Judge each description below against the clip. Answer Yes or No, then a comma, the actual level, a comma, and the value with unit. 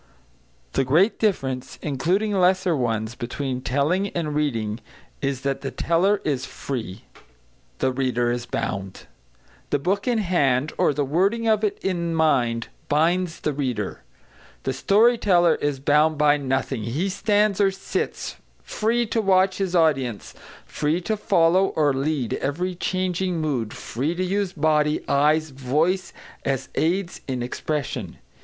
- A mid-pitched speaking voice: Yes, medium, 155 Hz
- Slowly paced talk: No, average, 145 wpm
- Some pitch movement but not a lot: No, wide, 5.7 semitones